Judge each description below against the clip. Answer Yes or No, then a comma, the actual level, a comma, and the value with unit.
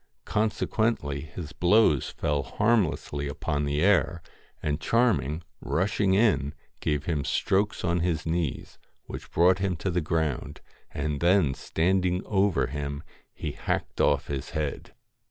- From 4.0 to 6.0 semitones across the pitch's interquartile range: Yes, average, 4.7 semitones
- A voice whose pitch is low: Yes, very low, 85 Hz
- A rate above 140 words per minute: No, slow, 135 wpm